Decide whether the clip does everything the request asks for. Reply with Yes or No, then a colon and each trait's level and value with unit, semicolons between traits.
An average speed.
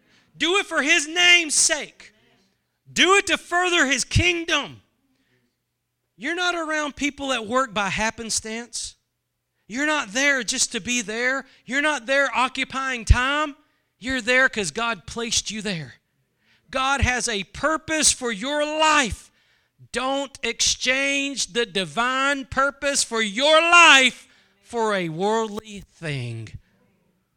No: slow, 125 wpm